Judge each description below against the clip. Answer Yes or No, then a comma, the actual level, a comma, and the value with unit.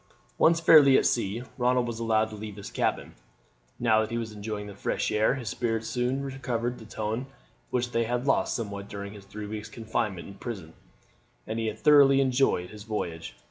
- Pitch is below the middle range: Yes, low, 110 Hz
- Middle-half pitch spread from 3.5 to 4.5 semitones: No, average, 2.7 semitones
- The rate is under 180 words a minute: No, average, 190 wpm